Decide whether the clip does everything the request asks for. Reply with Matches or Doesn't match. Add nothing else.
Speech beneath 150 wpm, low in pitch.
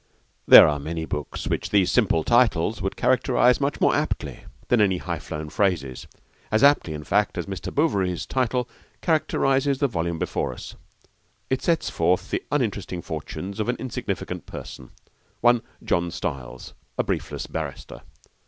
Doesn't match